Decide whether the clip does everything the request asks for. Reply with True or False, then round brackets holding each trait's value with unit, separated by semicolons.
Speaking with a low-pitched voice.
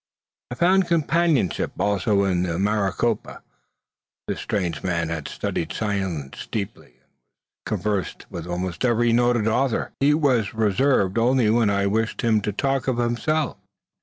True (110 Hz)